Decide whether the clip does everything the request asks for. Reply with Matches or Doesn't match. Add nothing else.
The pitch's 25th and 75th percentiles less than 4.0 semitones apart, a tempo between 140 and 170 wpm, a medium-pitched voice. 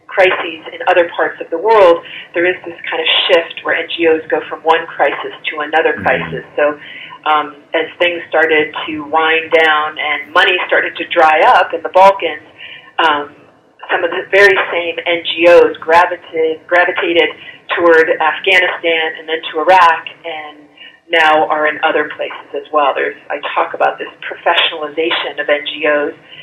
Matches